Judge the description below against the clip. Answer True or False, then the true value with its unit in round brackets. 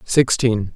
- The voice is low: True (115 Hz)